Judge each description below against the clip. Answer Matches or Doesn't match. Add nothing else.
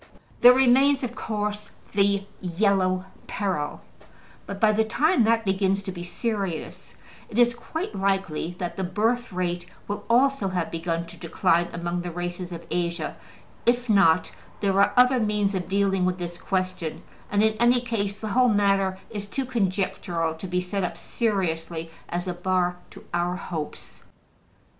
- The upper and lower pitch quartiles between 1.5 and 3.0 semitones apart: Doesn't match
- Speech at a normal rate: Matches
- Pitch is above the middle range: Matches